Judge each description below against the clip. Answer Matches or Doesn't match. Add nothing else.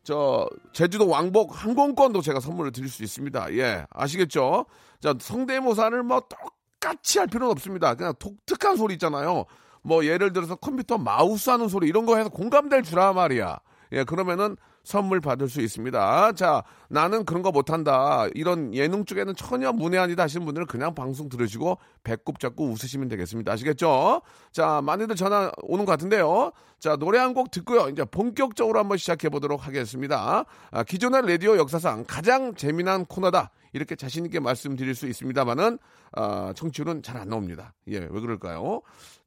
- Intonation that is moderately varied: Doesn't match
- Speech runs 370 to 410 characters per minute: Matches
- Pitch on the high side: Doesn't match